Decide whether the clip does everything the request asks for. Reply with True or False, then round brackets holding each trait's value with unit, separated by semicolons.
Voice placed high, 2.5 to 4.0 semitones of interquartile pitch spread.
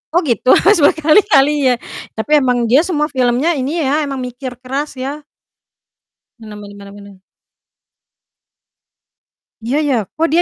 True (270 Hz; 3.6 semitones)